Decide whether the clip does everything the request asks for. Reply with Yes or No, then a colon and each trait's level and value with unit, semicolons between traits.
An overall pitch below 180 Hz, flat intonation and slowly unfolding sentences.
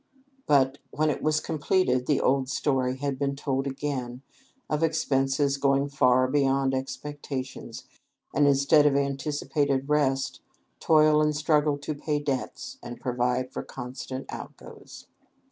Yes: medium, 140 Hz; narrow, 1.9 semitones; slow, 130 wpm